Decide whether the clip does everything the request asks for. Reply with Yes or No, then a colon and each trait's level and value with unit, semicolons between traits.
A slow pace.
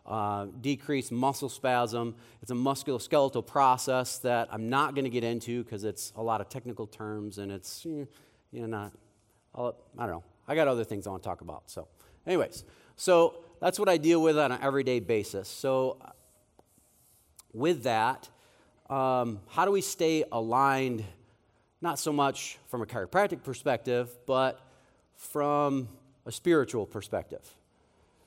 No: average, 160 wpm